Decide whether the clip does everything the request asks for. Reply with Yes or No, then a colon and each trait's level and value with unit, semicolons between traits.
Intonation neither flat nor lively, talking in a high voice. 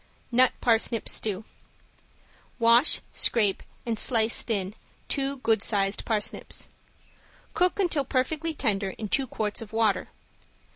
Yes: average, 3.6 semitones; high, 230 Hz